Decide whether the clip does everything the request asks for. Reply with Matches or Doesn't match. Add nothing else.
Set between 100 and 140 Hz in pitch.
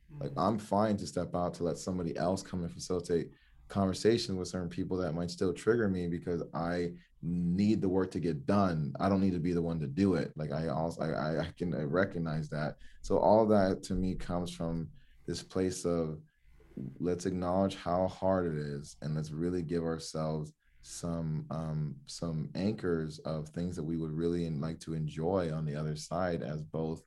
Doesn't match